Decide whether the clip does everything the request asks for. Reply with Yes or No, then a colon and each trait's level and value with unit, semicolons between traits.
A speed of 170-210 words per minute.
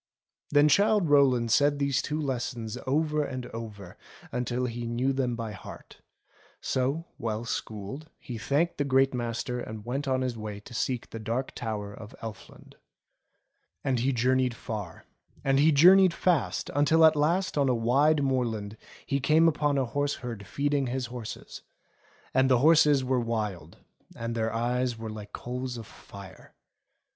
No: average, 160 wpm